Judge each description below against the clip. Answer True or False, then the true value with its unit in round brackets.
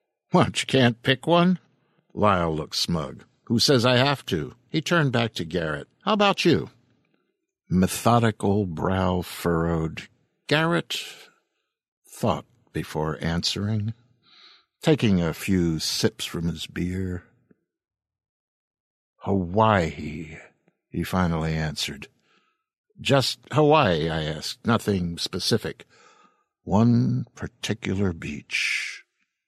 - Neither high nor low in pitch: False (100 Hz)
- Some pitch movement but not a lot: False (6.5 semitones)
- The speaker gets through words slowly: True (100 wpm)